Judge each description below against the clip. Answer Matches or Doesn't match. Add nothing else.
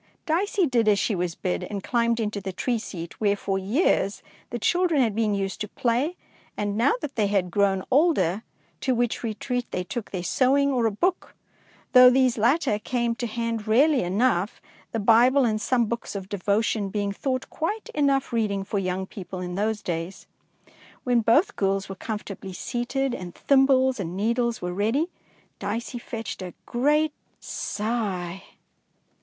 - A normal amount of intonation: Matches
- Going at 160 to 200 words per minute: Matches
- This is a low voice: Doesn't match